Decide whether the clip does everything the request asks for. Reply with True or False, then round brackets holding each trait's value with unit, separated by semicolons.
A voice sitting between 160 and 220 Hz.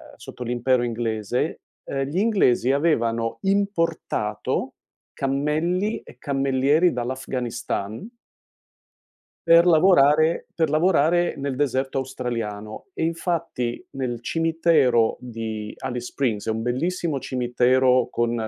False (130 Hz)